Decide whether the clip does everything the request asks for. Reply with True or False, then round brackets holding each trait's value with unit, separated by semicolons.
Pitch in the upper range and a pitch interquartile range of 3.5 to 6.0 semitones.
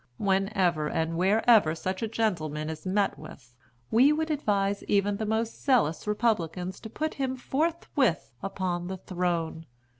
True (195 Hz; 4.7 semitones)